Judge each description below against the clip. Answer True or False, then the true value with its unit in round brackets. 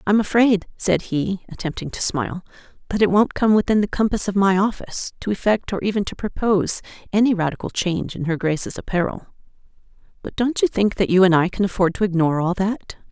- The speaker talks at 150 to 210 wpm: True (200 wpm)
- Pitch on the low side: False (195 Hz)